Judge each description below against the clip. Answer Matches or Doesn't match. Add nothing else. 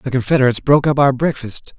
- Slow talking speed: Doesn't match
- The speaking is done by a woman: Doesn't match